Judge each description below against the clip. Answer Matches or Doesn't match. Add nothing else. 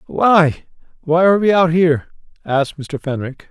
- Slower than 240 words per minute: Matches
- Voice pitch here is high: Doesn't match